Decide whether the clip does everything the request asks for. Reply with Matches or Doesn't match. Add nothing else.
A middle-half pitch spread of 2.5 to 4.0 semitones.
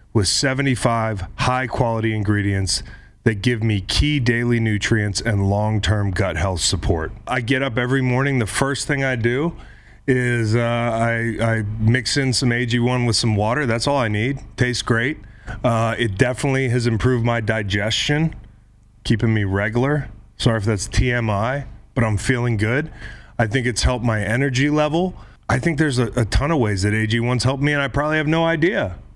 Matches